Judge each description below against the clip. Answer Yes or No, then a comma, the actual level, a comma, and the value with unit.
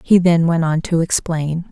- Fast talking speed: Yes, fast, 210 wpm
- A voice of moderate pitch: Yes, medium, 165 Hz